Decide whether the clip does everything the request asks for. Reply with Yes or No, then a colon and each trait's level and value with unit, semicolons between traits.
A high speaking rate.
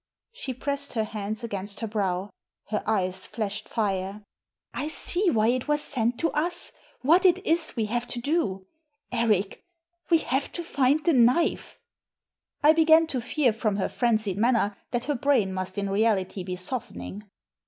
No: average, 170 wpm